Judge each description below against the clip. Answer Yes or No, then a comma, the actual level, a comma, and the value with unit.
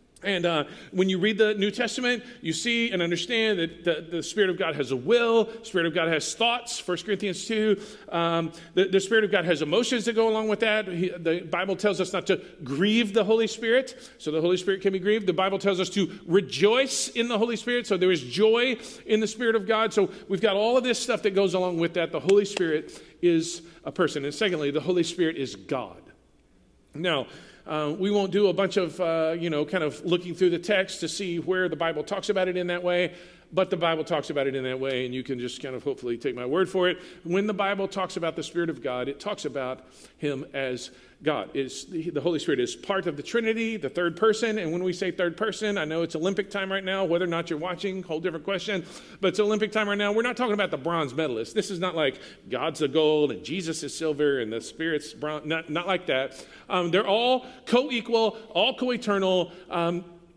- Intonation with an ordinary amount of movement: Yes, average, 4.3 semitones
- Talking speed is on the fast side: Yes, fast, 240 wpm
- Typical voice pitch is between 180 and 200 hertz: Yes, medium, 185 Hz